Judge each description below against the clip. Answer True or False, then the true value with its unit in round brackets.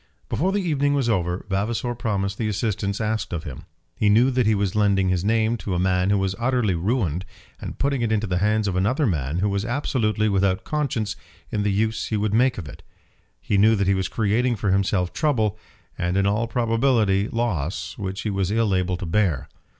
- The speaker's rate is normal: False (210 wpm)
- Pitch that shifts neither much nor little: True (3.2 semitones)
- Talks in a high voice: False (105 Hz)